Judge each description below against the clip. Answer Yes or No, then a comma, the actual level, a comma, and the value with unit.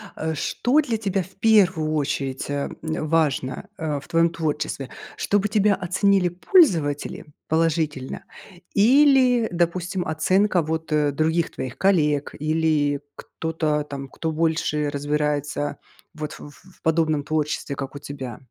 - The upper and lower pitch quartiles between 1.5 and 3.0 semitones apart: No, average, 3.8 semitones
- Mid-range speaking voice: Yes, medium, 160 Hz